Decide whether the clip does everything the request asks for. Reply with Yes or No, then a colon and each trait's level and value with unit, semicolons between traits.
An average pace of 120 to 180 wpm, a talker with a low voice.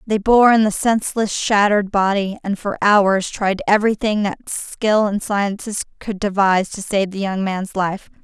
No: average, 175 wpm; high, 200 Hz